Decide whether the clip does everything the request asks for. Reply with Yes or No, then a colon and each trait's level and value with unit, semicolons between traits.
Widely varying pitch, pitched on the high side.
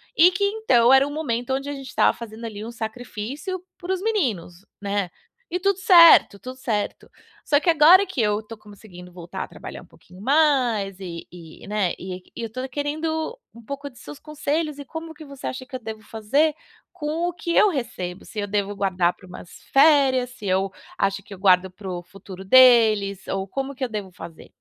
Yes: wide, 6.9 semitones; high, 235 Hz